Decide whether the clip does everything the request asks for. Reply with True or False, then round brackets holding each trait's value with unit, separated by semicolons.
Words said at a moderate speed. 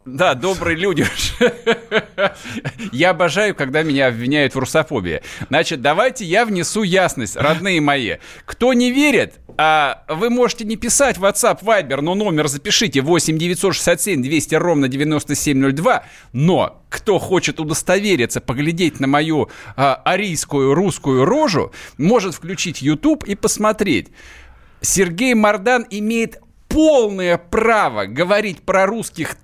True (120 wpm)